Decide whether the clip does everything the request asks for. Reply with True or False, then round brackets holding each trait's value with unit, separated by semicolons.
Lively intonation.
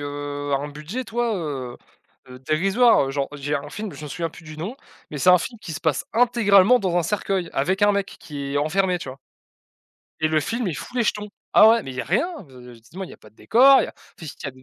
True (6.4 semitones)